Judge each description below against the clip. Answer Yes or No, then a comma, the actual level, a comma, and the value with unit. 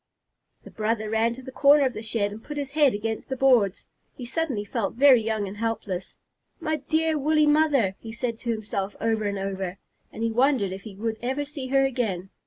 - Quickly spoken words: Yes, fast, 210 wpm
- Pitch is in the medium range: No, high, 230 Hz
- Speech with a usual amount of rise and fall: Yes, average, 4.5 semitones